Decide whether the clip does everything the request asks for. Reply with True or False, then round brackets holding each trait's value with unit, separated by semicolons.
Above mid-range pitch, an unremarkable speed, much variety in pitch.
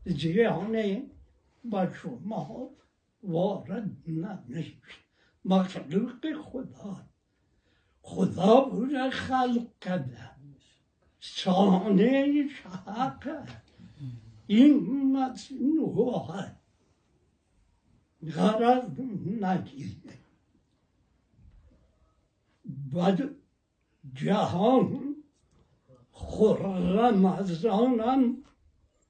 False (200 Hz; 45 wpm; 6.8 semitones)